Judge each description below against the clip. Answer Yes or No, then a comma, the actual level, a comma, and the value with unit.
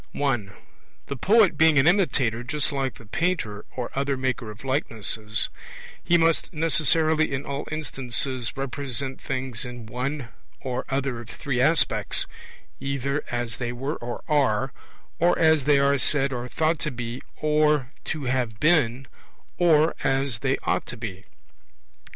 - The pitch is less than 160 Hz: Yes, low, 135 Hz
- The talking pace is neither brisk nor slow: Yes, average, 150 wpm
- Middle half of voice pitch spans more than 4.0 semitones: No, average, 3.7 semitones